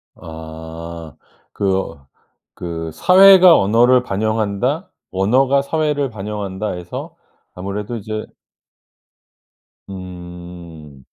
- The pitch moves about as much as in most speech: No, wide, 6.1 semitones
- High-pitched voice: No, low, 100 Hz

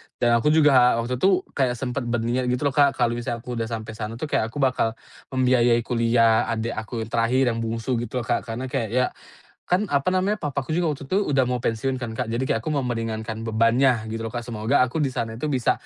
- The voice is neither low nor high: No, low, 120 Hz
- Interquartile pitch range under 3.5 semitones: Yes, narrow, 2.6 semitones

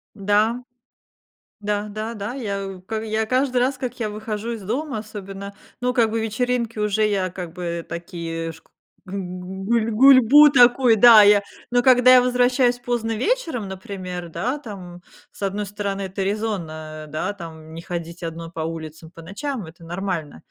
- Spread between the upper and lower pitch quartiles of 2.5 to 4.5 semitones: No, average, 5.0 semitones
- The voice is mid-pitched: No, high, 205 Hz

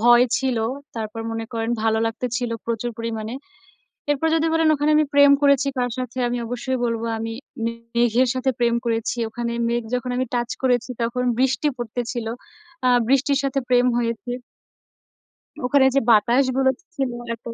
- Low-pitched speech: No, high, 245 Hz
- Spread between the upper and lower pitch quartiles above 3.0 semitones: No, narrow, 2.4 semitones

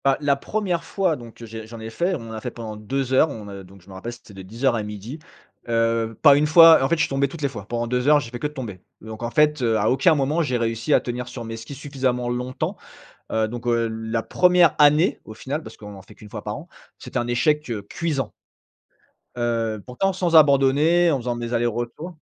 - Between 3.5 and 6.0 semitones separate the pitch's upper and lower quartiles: Yes, average, 4.7 semitones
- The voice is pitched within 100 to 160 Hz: Yes, low, 125 Hz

